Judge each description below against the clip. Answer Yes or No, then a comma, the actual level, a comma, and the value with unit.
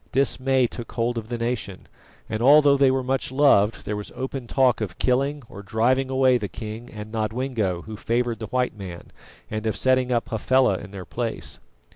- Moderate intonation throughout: Yes, average, 3.4 semitones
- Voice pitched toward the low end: Yes, low, 120 Hz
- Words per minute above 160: Yes, average, 190 wpm